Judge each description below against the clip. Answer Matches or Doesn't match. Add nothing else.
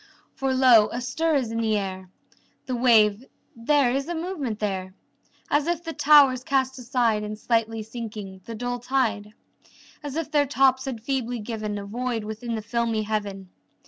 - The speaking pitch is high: Matches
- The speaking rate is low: Doesn't match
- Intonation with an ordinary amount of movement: Matches